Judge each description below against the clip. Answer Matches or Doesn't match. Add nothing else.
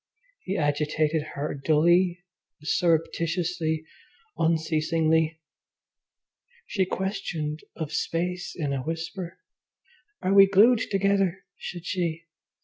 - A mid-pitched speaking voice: Matches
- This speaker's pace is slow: Matches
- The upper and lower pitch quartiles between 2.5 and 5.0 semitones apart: Matches